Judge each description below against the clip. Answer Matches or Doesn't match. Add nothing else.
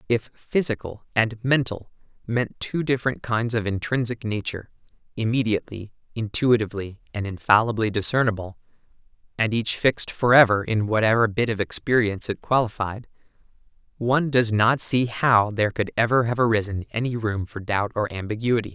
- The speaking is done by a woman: Doesn't match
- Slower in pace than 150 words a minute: Matches